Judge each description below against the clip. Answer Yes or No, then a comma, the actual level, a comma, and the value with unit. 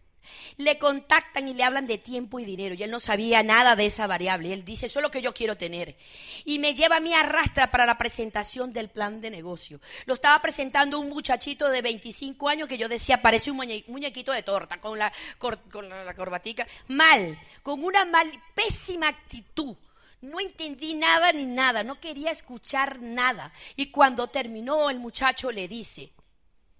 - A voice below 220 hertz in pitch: No, very high, 250 Hz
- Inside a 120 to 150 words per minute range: No, average, 185 wpm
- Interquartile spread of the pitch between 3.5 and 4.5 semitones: No, average, 5.1 semitones